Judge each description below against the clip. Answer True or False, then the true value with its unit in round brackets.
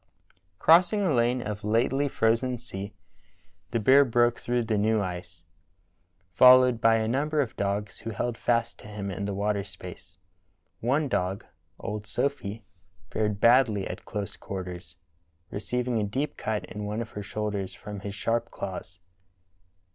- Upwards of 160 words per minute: False (155 wpm)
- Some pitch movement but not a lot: True (3.4 semitones)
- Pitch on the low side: True (110 Hz)